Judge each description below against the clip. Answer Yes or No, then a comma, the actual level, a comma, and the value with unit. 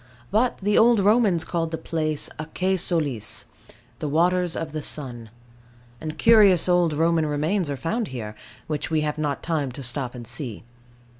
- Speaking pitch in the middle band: Yes, medium, 160 Hz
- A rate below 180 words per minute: Yes, average, 165 wpm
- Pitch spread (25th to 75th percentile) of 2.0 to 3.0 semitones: No, average, 3.9 semitones